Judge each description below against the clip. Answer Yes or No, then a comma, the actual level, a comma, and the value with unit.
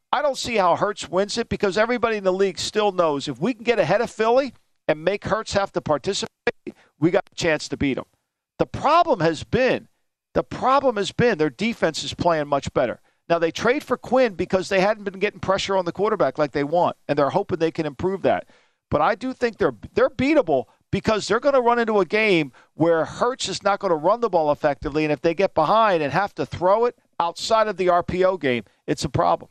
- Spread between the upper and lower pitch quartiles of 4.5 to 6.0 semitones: Yes, average, 5.0 semitones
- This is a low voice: No, high, 190 Hz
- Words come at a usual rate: No, fast, 235 wpm